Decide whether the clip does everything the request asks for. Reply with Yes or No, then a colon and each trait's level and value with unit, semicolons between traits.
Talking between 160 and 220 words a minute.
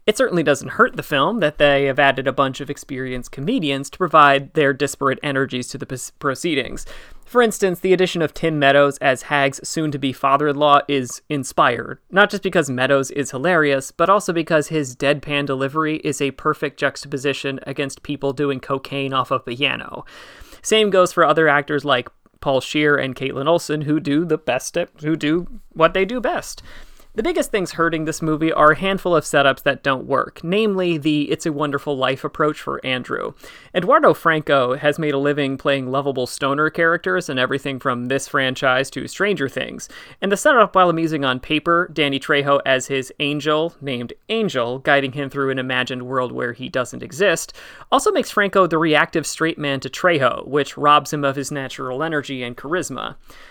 Yes: average, 185 wpm